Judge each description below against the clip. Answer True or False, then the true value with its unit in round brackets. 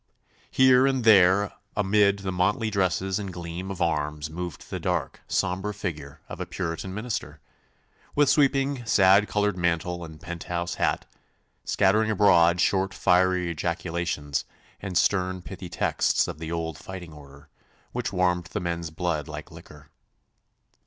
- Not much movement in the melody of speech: False (3.0 semitones)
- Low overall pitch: True (90 Hz)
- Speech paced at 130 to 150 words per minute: True (140 wpm)